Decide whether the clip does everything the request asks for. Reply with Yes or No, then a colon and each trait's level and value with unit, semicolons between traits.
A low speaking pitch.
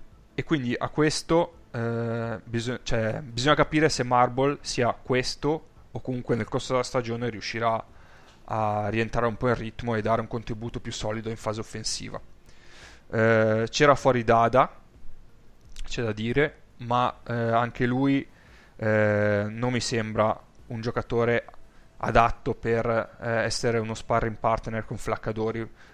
Yes: low, 115 Hz